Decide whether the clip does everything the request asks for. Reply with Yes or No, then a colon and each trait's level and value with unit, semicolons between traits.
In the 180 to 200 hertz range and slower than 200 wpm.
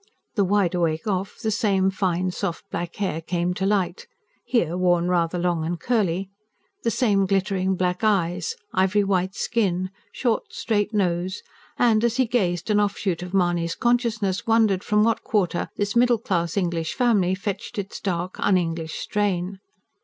Yes: high, 190 Hz; average, 160 wpm